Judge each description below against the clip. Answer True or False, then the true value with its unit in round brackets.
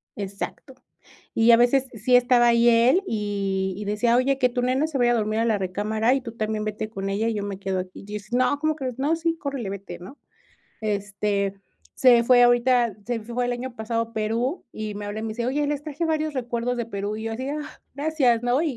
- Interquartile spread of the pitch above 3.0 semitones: True (3.5 semitones)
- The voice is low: False (235 Hz)